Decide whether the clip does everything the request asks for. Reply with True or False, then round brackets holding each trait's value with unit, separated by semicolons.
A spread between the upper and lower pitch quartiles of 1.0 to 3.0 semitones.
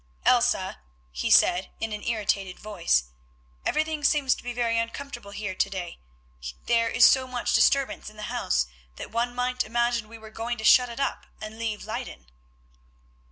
True (2.7 semitones)